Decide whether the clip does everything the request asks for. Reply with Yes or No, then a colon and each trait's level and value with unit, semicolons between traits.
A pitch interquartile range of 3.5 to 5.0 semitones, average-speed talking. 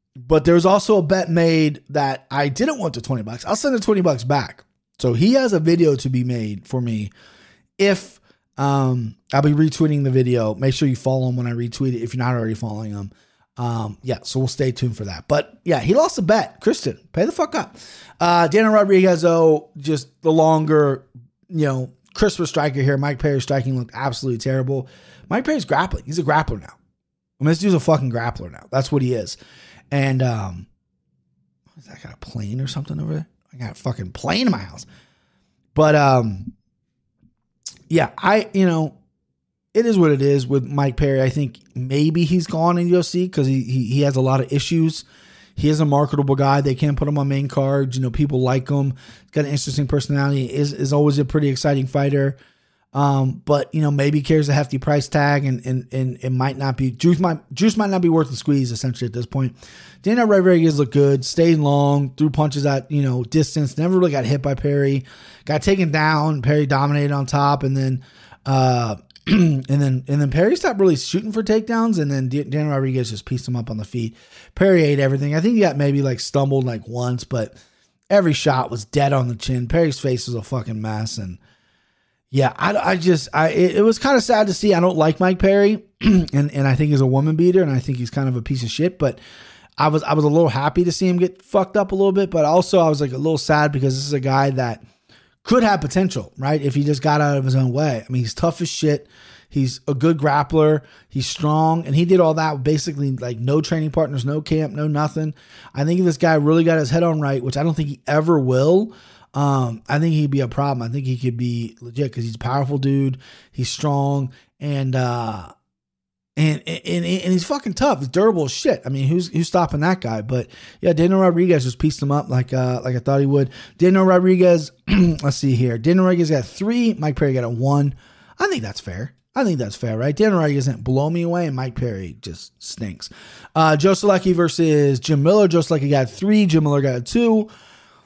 No: average, 4.2 semitones; fast, 225 wpm